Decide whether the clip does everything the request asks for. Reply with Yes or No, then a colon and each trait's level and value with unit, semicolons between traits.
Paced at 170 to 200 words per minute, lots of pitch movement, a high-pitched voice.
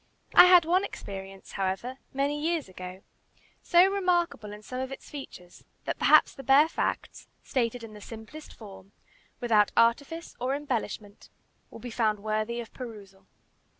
No: average, 150 wpm; wide, 5.9 semitones; high, 235 Hz